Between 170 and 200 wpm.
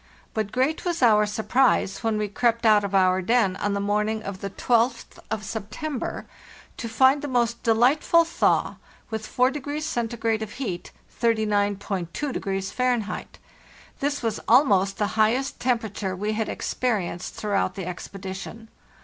No: average, 140 wpm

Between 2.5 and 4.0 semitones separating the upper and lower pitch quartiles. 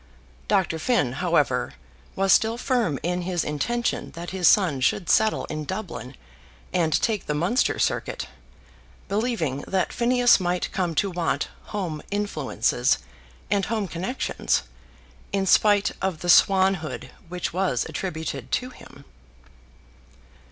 No: average, 4.7 semitones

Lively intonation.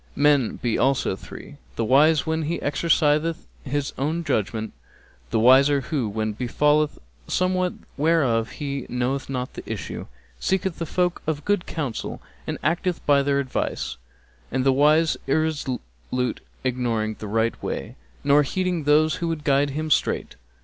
No: average, 4.0 semitones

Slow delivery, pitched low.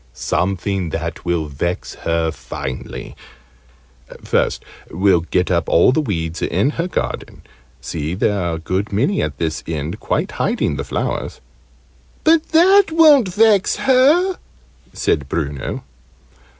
Yes: slow, 130 wpm; very low, 95 Hz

